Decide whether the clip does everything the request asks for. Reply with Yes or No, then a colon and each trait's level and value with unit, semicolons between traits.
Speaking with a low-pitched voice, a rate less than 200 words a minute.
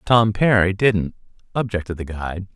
Yes: low, 100 Hz; average, 140 wpm